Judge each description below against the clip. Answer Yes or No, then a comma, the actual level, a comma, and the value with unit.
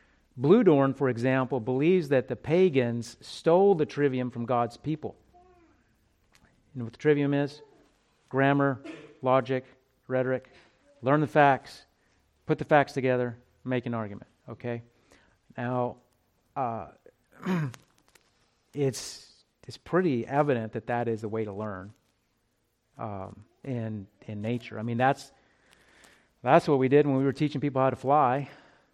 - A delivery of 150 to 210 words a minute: No, slow, 135 wpm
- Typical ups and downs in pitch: Yes, average, 3.2 semitones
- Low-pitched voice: Yes, low, 130 Hz